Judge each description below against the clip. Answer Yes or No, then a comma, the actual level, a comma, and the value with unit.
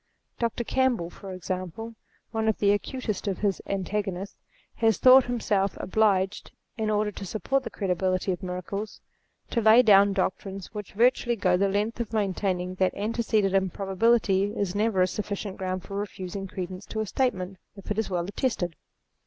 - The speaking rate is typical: Yes, average, 170 wpm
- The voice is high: Yes, high, 200 Hz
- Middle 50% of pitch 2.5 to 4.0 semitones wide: Yes, average, 2.8 semitones